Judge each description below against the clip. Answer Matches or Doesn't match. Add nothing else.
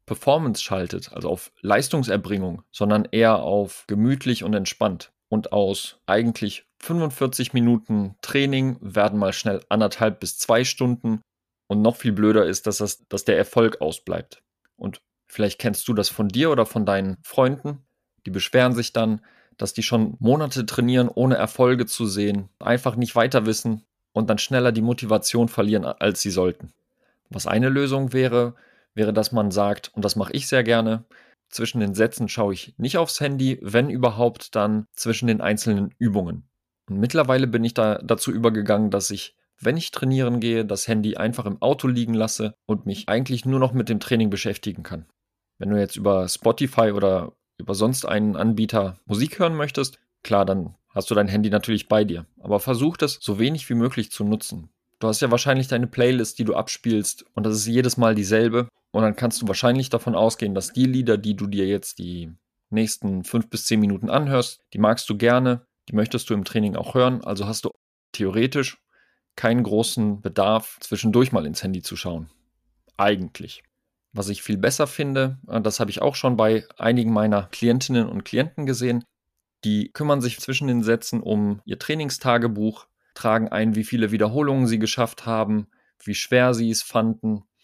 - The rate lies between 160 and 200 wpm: Matches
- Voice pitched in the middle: Doesn't match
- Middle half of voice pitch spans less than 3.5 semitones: Matches